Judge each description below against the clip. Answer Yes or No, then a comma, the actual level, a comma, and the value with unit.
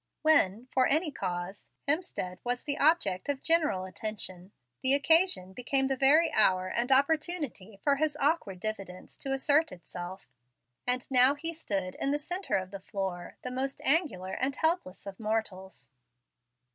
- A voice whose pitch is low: No, very high, 255 Hz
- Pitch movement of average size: No, wide, 7.6 semitones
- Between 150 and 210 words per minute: Yes, average, 155 wpm